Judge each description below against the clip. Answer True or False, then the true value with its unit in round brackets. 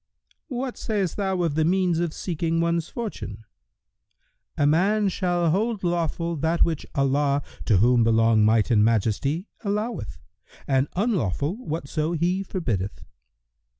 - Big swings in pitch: True (5.9 semitones)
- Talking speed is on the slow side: True (130 wpm)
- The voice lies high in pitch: False (165 Hz)